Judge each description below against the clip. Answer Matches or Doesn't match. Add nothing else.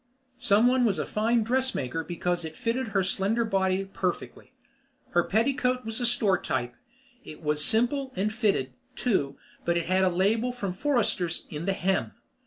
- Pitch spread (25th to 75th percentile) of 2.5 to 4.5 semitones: Doesn't match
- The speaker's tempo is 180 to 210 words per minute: Doesn't match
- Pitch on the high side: Matches